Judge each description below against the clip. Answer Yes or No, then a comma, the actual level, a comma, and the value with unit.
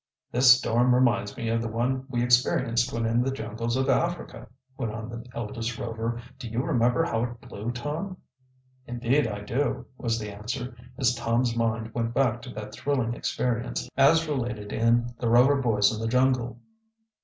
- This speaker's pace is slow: No, average, 180 wpm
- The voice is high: No, low, 120 Hz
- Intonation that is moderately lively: No, narrow, 1.8 semitones